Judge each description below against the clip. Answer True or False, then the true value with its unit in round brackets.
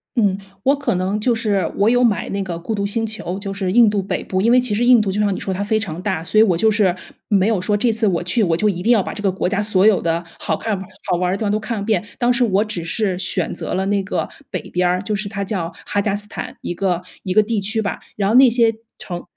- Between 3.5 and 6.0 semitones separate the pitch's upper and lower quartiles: False (2.8 semitones)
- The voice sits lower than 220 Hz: True (200 Hz)